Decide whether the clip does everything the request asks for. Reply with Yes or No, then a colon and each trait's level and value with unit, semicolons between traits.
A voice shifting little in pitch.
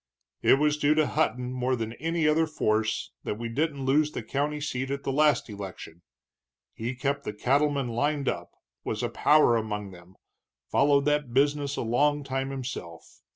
No: average, 4.1 semitones